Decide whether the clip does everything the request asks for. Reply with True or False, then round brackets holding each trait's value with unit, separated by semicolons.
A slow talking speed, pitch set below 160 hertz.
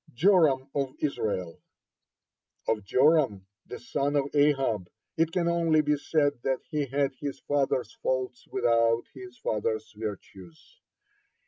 True (130 wpm; 135 Hz)